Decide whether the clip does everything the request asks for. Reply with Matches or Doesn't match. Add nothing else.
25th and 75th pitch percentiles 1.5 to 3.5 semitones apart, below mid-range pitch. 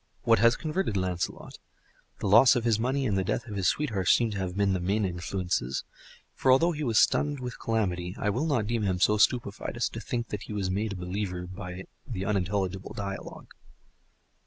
Doesn't match